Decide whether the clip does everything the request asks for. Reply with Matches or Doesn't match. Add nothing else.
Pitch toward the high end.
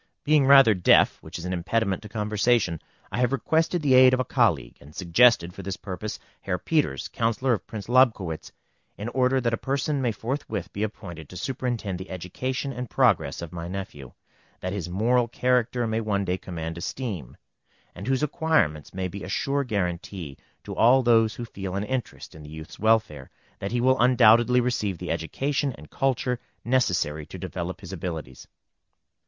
Doesn't match